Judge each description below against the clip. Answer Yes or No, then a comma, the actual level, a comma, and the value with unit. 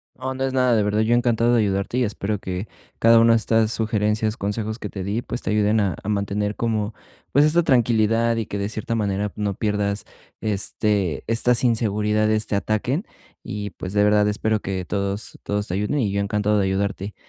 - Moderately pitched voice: No, low, 105 Hz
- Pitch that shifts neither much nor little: No, narrow, 2.1 semitones